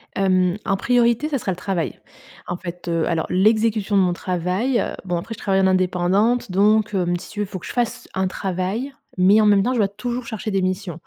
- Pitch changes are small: No, average, 3.2 semitones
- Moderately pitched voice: No, high, 195 Hz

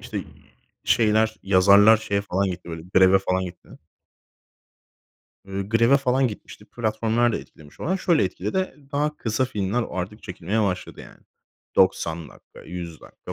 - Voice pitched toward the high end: No, low, 105 Hz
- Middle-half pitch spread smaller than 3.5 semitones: No, average, 3.9 semitones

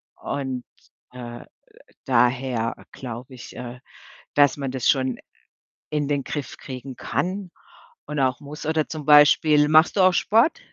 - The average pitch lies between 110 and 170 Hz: Yes, medium, 140 Hz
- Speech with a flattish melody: No, average, 3.0 semitones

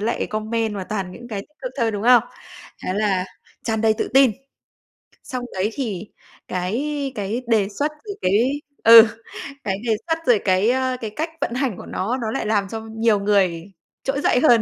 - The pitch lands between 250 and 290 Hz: No, high, 225 Hz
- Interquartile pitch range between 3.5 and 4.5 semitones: Yes, average, 3.8 semitones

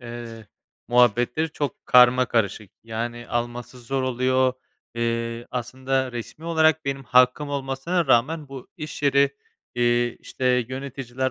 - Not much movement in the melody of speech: Yes, narrow, 2.3 semitones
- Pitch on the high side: No, low, 125 Hz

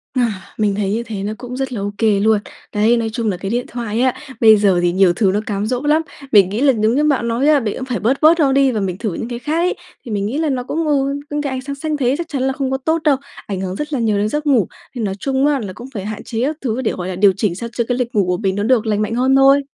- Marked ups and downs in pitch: No, average, 4.6 semitones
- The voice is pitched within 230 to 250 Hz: Yes, high, 235 Hz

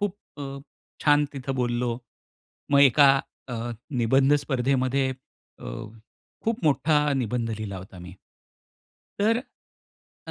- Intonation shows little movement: No, average, 3.5 semitones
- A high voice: No, low, 130 Hz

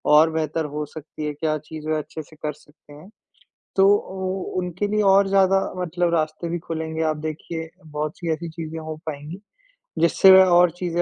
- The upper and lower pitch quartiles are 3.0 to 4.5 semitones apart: No, narrow, 2.4 semitones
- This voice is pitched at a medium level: Yes, medium, 160 Hz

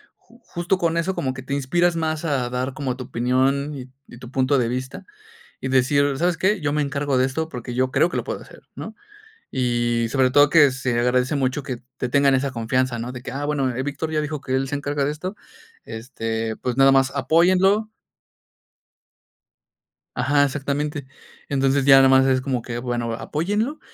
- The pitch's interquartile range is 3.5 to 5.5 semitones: No, average, 2.7 semitones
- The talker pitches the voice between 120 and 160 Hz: Yes, low, 135 Hz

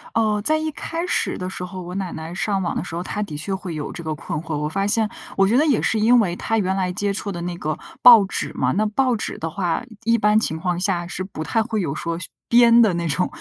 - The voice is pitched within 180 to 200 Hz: Yes, high, 195 Hz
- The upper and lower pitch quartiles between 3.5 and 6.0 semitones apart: Yes, average, 4.3 semitones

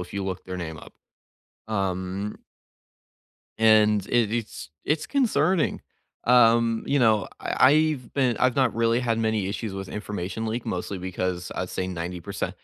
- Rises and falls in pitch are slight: No, average, 4.2 semitones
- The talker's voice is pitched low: Yes, low, 110 Hz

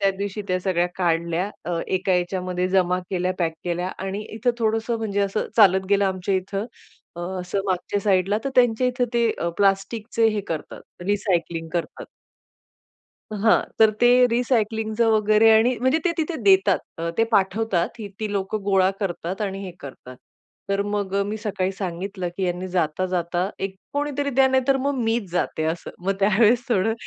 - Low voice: No, high, 195 Hz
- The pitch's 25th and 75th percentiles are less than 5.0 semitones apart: Yes, average, 3.3 semitones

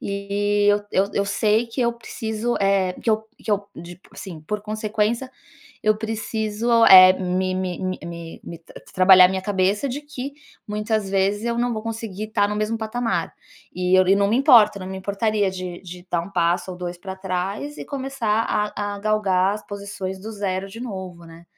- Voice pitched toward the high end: Yes, high, 200 Hz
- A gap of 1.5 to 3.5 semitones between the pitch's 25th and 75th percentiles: Yes, average, 2.8 semitones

